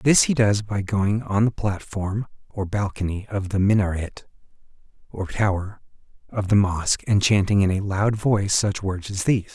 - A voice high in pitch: No, low, 100 Hz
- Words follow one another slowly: No, average, 175 wpm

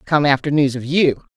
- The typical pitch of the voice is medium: Yes, medium, 145 Hz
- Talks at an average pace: No, fast, 220 wpm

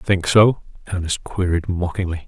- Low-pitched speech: Yes, very low, 90 Hz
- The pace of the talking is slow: Yes, slow, 130 wpm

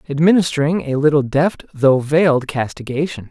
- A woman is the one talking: No, male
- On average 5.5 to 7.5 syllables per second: No, 5.2 syllables/s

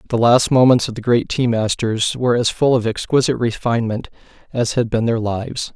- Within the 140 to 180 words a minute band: No, average, 200 wpm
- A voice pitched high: No, low, 120 Hz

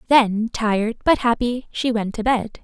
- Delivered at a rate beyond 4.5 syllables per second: No, 4.3 syllables/s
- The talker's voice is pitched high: Yes, high, 230 Hz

